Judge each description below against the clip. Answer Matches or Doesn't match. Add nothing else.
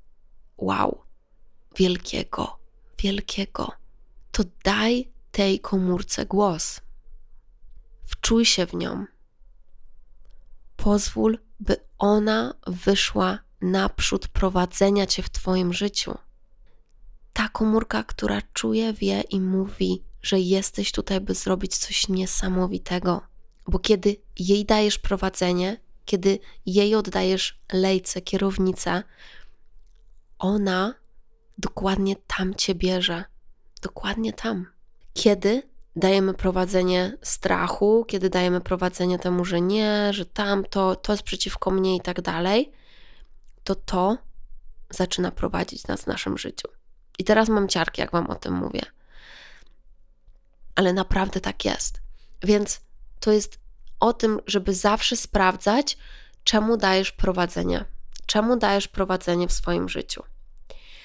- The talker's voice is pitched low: Doesn't match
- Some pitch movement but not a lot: Doesn't match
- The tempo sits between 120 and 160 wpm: Doesn't match